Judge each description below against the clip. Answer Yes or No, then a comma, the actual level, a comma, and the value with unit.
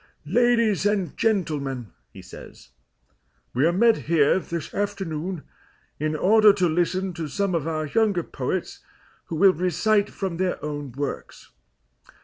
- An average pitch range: Yes, average, 4.6 semitones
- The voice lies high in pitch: No, medium, 180 Hz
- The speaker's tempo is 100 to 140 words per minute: Yes, slow, 135 wpm